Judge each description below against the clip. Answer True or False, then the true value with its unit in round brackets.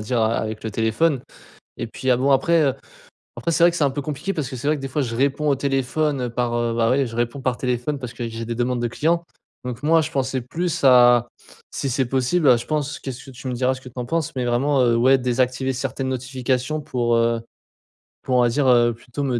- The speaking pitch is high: False (130 Hz)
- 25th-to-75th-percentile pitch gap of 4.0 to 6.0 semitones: False (2.8 semitones)